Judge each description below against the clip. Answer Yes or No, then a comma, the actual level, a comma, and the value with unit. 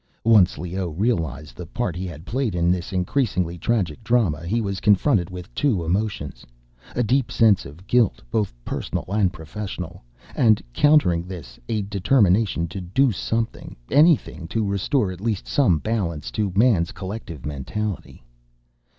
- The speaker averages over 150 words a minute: No, average, 145 wpm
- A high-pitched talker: No, very low, 95 Hz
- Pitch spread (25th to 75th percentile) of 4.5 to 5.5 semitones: Yes, average, 4.9 semitones